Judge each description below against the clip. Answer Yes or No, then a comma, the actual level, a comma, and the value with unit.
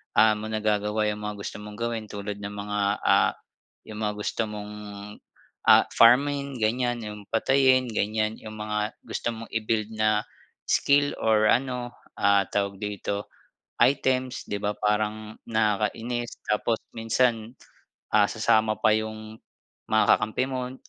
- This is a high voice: No, low, 110 Hz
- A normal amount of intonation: No, narrow, 1.9 semitones